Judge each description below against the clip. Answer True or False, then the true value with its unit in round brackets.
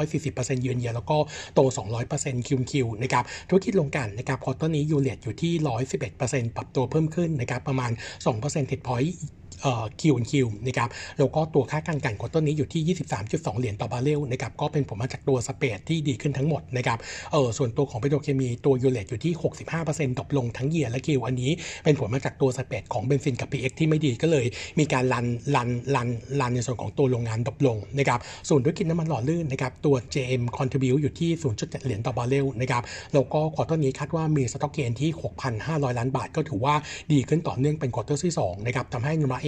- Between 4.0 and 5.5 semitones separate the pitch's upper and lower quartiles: False (3.0 semitones)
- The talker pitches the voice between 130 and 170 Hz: True (135 Hz)